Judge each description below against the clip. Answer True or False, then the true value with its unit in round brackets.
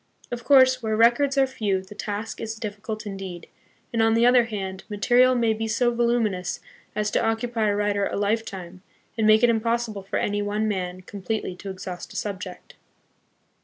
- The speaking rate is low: False (180 wpm)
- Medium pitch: False (215 Hz)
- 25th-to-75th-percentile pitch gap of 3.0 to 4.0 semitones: False (2.6 semitones)